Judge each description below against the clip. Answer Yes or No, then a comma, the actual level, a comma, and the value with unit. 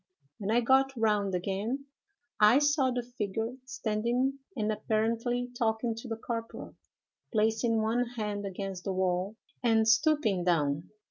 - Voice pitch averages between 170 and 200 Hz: No, high, 220 Hz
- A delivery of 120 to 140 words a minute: Yes, slow, 135 wpm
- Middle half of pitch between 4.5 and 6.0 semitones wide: No, average, 3.0 semitones